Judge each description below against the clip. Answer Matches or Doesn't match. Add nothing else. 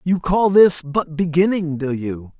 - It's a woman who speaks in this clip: Doesn't match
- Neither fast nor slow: Matches